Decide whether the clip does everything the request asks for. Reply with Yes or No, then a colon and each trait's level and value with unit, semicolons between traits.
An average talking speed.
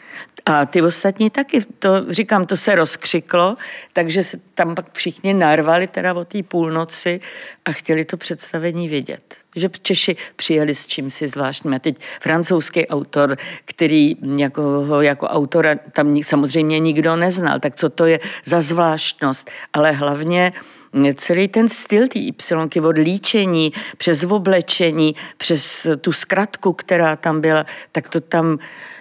Yes: average, 145 wpm